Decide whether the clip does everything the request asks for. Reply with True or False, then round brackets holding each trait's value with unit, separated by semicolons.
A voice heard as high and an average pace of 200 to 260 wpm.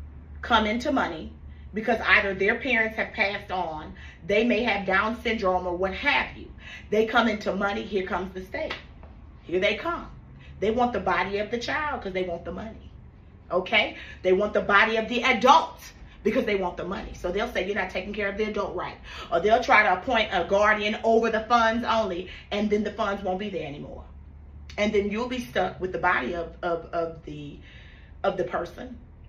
True (200 Hz; 205 wpm)